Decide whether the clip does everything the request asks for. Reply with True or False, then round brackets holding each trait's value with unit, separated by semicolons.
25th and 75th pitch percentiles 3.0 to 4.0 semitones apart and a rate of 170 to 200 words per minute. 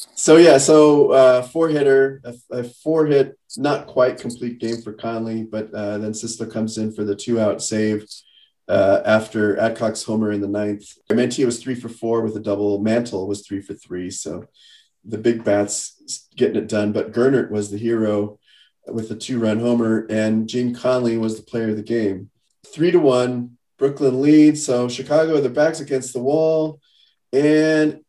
True (3.6 semitones; 185 wpm)